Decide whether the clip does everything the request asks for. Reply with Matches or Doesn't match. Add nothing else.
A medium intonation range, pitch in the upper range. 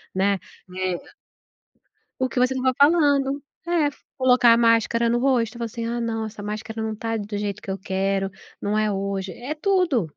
Matches